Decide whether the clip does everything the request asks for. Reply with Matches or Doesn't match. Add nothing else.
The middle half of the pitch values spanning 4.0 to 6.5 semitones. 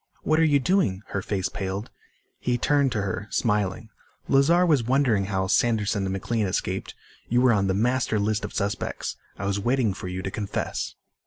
Matches